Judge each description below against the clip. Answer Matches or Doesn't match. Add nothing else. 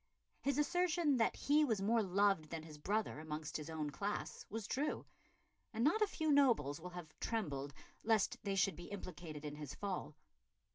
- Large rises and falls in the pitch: Matches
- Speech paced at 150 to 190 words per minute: Matches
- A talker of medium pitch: Doesn't match